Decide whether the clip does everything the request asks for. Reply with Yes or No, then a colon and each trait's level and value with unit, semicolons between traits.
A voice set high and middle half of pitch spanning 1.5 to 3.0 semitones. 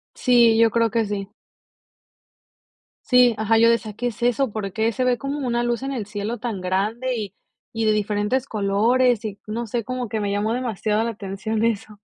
Yes: high, 225 Hz; narrow, 2.6 semitones